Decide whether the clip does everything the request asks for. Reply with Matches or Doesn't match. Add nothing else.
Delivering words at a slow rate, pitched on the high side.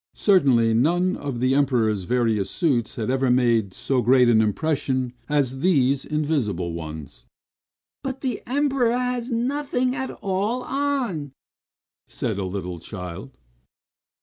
Doesn't match